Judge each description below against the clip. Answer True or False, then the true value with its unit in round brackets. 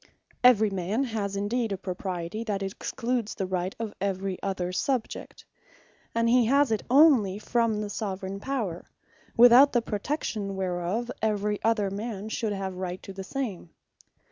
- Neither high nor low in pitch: False (205 Hz)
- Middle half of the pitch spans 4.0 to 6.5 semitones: False (3.4 semitones)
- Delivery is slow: False (155 wpm)